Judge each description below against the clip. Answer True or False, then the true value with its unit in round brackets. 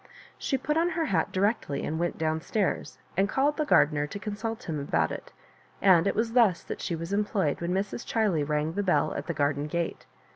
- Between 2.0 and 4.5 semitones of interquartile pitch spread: False (5.5 semitones)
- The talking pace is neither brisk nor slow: False (215 wpm)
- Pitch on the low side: False (185 Hz)